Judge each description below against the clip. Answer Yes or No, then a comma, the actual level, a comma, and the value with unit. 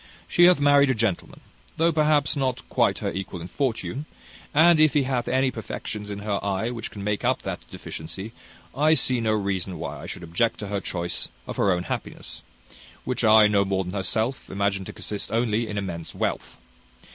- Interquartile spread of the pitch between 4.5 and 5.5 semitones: Yes, average, 5.2 semitones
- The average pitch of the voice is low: Yes, low, 110 Hz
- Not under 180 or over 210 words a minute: Yes, average, 195 wpm